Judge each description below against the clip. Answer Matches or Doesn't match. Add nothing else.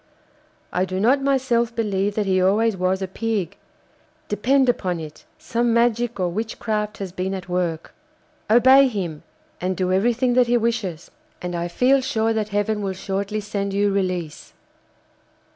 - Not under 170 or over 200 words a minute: Doesn't match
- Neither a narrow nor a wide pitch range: Matches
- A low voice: Doesn't match